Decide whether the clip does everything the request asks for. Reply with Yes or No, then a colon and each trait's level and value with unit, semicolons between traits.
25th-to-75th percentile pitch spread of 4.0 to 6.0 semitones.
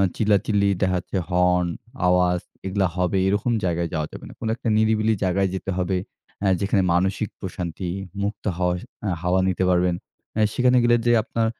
No: narrow, 2.6 semitones